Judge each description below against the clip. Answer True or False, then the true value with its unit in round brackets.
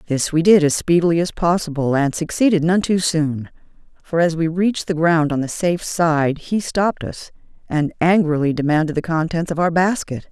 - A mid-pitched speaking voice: True (165 Hz)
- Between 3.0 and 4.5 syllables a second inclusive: False (5.2 syllables/s)